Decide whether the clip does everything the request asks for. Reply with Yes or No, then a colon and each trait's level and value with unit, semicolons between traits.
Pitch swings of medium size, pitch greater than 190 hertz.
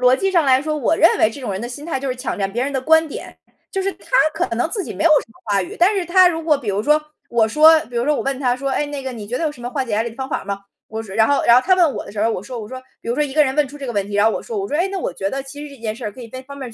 Yes: average, 4.9 semitones; very high, 265 Hz